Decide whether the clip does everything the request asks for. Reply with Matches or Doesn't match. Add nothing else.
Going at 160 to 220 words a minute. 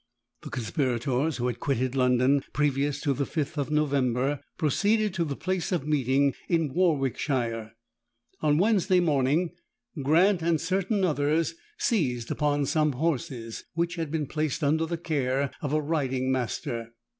Doesn't match